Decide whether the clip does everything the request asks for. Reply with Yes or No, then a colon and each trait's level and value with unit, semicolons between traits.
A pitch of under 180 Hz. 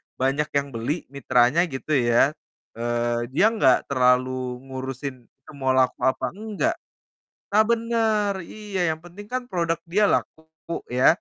Yes: medium, 140 Hz